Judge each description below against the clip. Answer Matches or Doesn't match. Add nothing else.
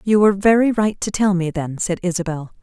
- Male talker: Doesn't match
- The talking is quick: Matches